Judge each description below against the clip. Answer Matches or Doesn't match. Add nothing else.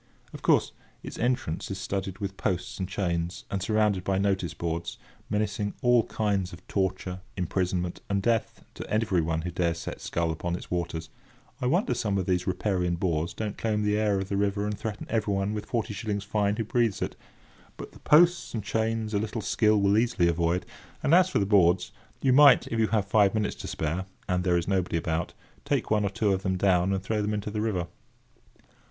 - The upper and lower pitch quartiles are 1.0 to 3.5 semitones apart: Matches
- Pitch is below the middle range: Matches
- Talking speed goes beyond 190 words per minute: Matches